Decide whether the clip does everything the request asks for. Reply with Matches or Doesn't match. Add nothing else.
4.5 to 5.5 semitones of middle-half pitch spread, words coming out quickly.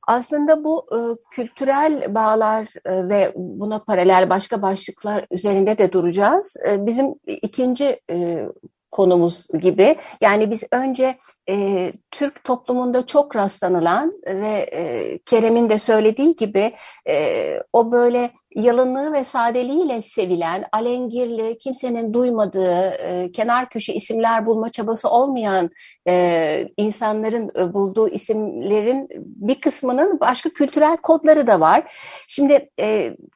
Doesn't match